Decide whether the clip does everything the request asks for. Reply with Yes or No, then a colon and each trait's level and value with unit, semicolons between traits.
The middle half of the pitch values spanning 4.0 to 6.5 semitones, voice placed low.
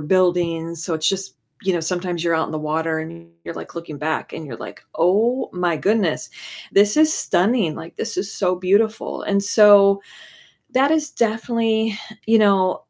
No: average, 4.3 semitones; medium, 185 Hz